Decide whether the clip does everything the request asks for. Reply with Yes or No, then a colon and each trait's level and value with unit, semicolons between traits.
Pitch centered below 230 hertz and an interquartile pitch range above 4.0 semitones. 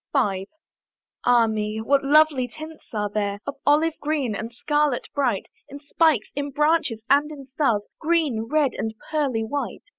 No: very high, 275 Hz; average, 5.1 semitones